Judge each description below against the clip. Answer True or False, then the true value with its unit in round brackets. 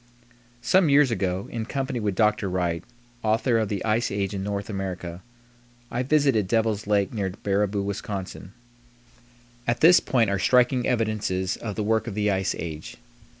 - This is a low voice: True (105 Hz)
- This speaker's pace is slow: False (160 wpm)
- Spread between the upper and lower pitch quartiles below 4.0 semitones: True (3.2 semitones)